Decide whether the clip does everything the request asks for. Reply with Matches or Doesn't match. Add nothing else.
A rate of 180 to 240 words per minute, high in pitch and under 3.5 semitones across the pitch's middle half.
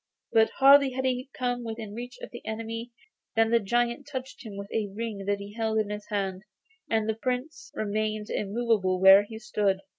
Matches